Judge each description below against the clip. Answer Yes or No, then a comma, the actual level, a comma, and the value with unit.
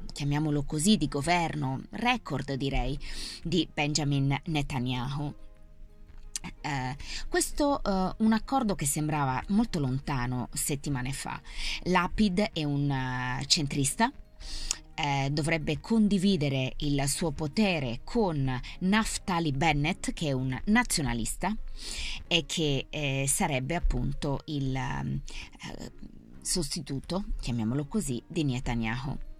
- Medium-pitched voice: Yes, medium, 145 Hz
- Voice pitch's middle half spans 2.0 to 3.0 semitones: No, average, 5.2 semitones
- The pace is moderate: No, slow, 100 wpm